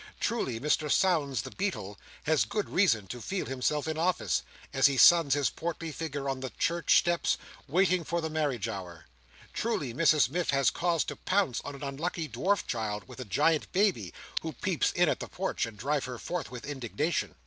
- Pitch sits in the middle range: Yes, medium, 145 Hz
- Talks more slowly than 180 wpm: No, average, 190 wpm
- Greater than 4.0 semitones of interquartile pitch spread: Yes, average, 5.2 semitones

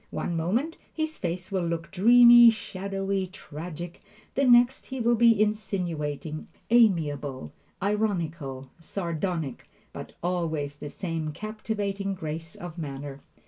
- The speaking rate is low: Yes, slow, 115 wpm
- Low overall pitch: No, medium, 180 Hz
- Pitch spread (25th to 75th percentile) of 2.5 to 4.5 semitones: No, average, 5.3 semitones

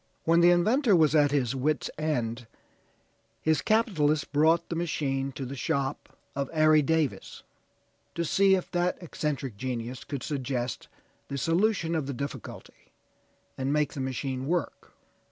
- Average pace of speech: Yes, average, 145 wpm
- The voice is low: No, medium, 150 Hz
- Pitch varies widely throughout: No, average, 3.8 semitones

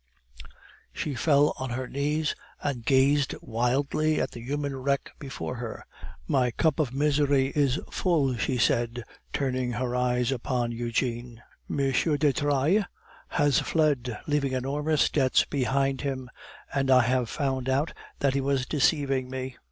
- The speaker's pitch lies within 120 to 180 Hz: Yes, low, 135 Hz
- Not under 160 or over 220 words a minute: No, average, 145 wpm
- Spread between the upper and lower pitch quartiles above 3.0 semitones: No, narrow, 2.5 semitones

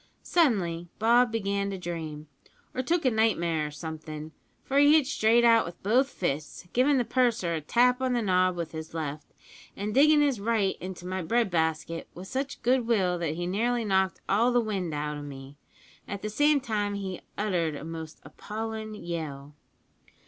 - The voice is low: No, high, 195 Hz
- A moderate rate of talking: Yes, average, 185 wpm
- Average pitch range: No, wide, 6.3 semitones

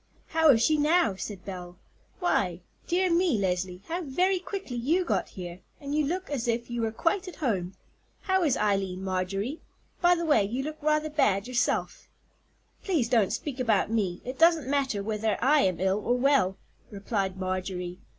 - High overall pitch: Yes, high, 240 Hz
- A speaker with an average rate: Yes, average, 180 wpm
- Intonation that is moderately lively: No, wide, 8.1 semitones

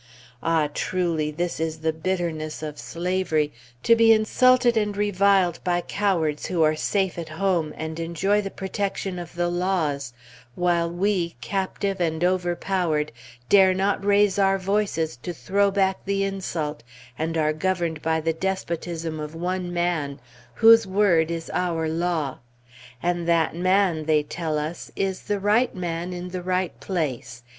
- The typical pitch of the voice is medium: Yes, medium, 175 Hz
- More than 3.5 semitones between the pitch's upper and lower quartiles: No, average, 3.2 semitones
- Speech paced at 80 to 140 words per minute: No, average, 150 wpm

